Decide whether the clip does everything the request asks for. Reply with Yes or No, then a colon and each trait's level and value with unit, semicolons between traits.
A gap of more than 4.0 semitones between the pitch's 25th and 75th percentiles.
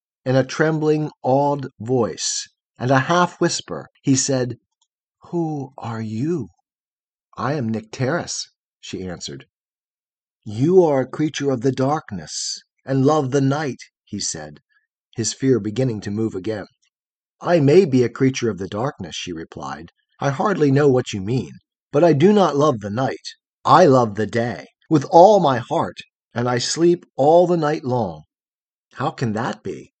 Yes: average, 5.0 semitones